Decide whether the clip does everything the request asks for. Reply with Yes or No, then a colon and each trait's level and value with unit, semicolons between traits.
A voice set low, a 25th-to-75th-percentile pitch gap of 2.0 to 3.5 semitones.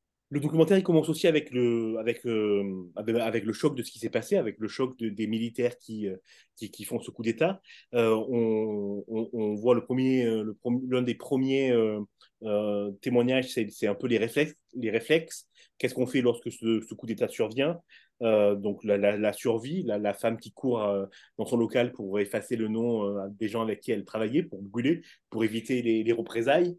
Yes: low, 115 Hz; narrow, 2.6 semitones